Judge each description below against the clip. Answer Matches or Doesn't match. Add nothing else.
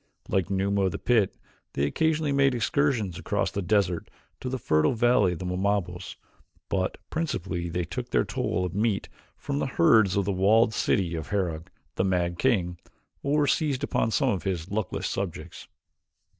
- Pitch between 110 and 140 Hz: Doesn't match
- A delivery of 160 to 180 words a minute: Matches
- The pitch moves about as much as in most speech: Matches